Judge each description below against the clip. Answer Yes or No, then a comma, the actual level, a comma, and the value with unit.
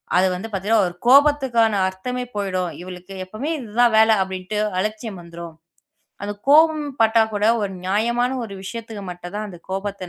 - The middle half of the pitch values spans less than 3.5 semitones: No, average, 3.9 semitones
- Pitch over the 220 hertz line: No, high, 210 Hz